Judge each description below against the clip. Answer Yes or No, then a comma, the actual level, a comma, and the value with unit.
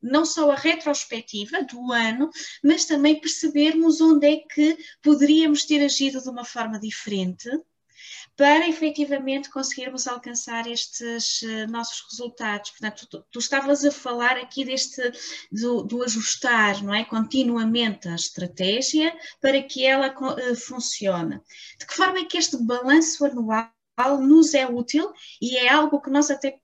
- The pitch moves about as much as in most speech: Yes, average, 4.0 semitones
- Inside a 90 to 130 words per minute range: No, average, 145 wpm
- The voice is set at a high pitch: Yes, very high, 265 Hz